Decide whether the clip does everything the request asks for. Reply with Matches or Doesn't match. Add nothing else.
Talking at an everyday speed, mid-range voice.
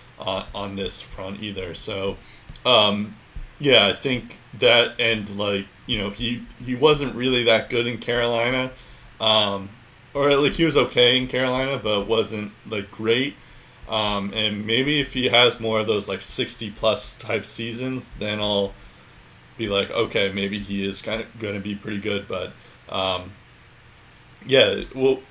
Doesn't match